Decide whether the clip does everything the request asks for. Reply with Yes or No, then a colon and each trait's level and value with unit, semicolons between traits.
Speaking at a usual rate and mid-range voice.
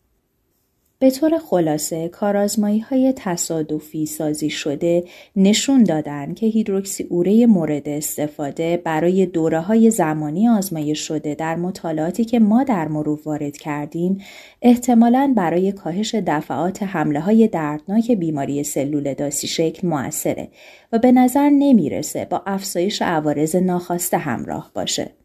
Yes: average, 120 wpm; medium, 175 Hz